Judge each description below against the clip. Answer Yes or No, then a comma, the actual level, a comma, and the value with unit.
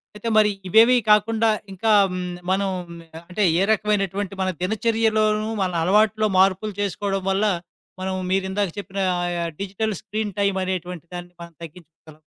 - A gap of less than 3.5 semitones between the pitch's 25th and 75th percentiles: Yes, narrow, 2.6 semitones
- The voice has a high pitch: Yes, high, 200 Hz